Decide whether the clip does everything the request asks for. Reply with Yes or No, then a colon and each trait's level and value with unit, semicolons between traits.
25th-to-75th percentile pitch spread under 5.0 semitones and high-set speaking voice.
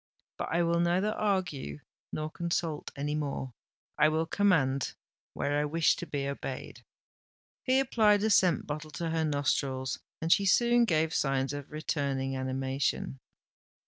No: average, 4.0 semitones; medium, 155 Hz